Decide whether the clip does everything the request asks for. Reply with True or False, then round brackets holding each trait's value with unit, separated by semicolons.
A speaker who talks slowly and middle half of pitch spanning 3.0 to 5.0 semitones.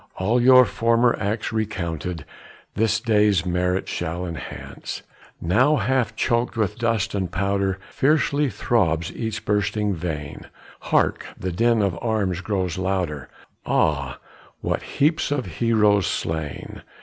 True (125 wpm; 4.4 semitones)